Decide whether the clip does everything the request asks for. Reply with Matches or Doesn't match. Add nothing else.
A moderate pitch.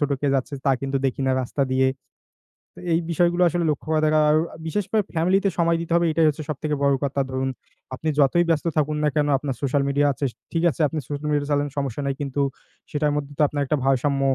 Matches